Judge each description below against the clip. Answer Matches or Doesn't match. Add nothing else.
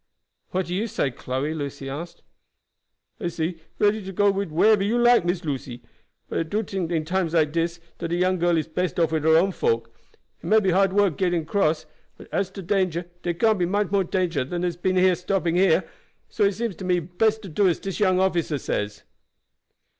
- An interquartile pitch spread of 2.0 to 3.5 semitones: Matches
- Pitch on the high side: Doesn't match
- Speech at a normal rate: Doesn't match